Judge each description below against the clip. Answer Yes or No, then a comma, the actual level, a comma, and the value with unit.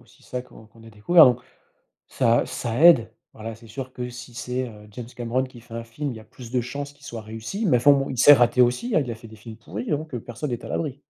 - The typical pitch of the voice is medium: No, low, 125 Hz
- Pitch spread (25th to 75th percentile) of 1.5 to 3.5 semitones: Yes, average, 2.8 semitones